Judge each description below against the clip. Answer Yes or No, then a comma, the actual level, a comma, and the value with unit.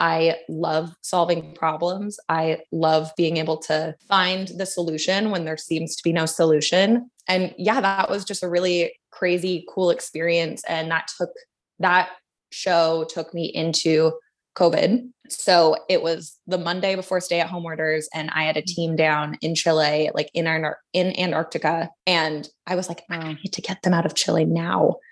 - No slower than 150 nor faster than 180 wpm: Yes, average, 175 wpm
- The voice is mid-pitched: Yes, medium, 165 Hz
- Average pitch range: No, narrow, 2.3 semitones